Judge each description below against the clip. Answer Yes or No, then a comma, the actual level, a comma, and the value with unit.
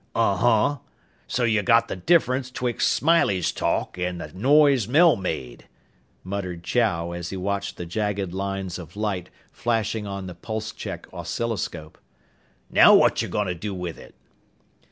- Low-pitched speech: Yes, low, 100 Hz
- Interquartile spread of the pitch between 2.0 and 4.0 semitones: No, average, 4.5 semitones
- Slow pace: No, average, 155 wpm